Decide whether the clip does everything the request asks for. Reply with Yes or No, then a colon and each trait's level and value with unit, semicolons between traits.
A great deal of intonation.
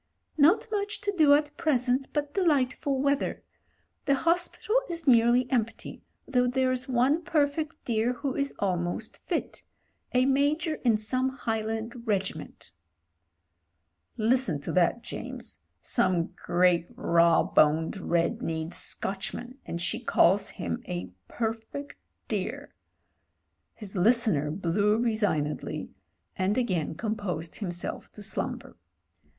Yes: wide, 6.9 semitones